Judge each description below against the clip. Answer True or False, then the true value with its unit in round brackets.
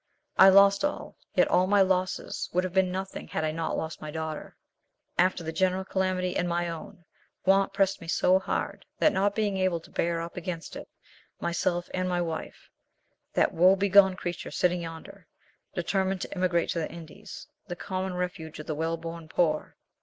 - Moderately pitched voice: True (180 Hz)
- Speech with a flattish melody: True (2.2 semitones)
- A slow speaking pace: False (180 wpm)